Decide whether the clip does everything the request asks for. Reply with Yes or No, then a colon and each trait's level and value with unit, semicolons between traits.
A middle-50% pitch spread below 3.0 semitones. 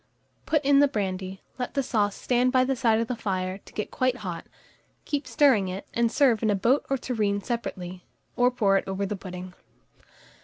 No: average, 4.8 semitones